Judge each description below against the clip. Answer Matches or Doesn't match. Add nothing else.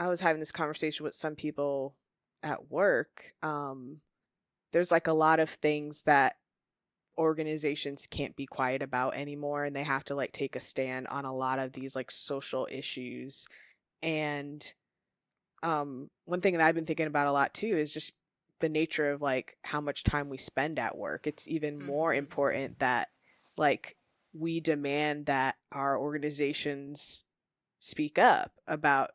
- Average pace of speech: Matches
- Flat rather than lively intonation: Matches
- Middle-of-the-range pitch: Matches